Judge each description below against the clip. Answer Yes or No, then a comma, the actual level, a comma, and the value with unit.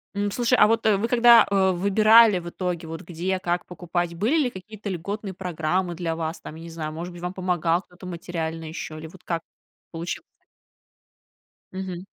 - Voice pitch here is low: No, medium, 180 Hz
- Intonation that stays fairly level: No, average, 3.1 semitones